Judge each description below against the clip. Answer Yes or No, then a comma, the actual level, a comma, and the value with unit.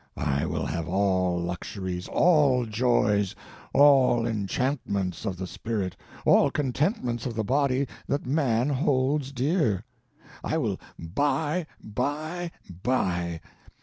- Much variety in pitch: Yes, wide, 7.0 semitones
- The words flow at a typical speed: No, slow, 115 wpm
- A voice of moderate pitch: No, low, 120 Hz